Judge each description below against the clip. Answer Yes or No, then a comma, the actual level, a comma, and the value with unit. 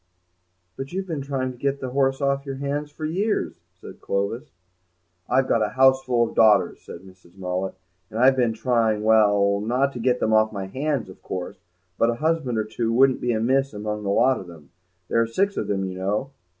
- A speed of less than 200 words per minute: No, fast, 205 wpm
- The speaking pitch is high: No, low, 120 Hz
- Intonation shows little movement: No, average, 4.5 semitones